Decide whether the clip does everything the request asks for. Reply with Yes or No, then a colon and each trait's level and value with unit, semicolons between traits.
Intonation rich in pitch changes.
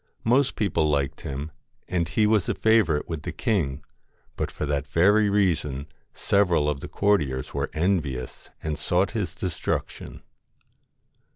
Yes: wide, 5.7 semitones